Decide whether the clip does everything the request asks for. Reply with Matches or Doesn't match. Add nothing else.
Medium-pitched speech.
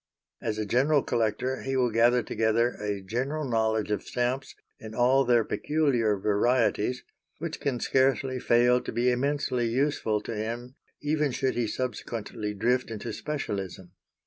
Doesn't match